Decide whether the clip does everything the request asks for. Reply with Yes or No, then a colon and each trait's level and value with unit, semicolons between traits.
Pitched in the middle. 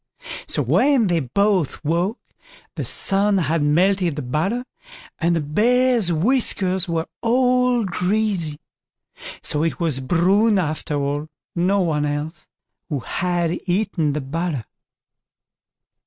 Yes: medium, 175 Hz